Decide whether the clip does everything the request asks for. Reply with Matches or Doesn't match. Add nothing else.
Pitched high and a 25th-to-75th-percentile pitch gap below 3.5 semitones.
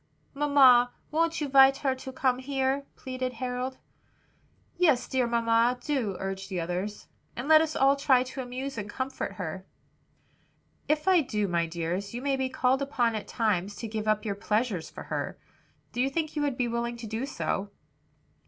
Doesn't match